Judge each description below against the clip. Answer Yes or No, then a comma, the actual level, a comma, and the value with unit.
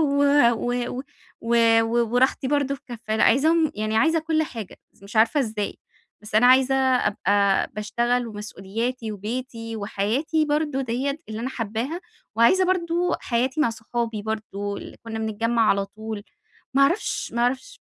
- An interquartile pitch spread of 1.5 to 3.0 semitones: No, average, 3.9 semitones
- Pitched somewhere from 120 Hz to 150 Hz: No, high, 235 Hz